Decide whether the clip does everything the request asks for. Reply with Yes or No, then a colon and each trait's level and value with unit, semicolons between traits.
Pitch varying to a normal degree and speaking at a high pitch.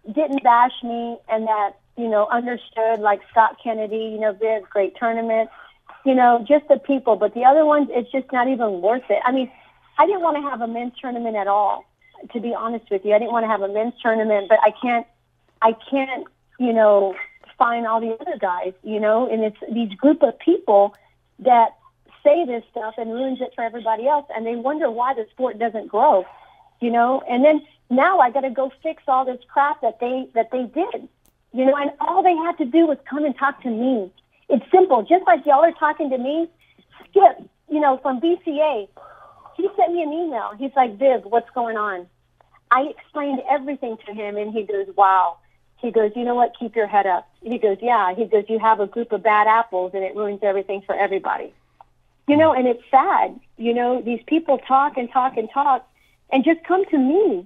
Yes: average, 4.2 semitones; high, 240 Hz